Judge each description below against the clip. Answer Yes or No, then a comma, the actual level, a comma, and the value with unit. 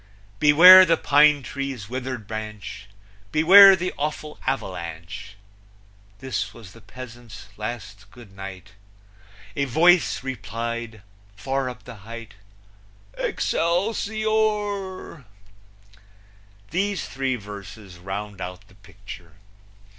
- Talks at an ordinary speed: No, slow, 95 wpm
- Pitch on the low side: Yes, low, 120 Hz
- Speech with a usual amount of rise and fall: No, wide, 7.0 semitones